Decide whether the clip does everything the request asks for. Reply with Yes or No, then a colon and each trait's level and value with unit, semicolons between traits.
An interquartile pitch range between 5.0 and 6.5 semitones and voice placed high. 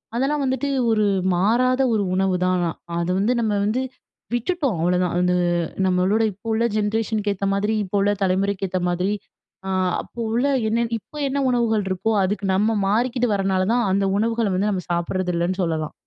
No: average, 3.8 semitones; high, 205 Hz